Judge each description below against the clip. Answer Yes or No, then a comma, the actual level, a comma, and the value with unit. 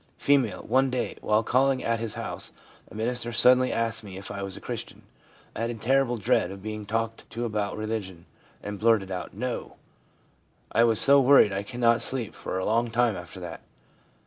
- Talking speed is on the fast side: Yes, fast, 210 wpm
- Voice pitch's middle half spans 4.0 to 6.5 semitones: No, average, 3.1 semitones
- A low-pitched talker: Yes, low, 115 Hz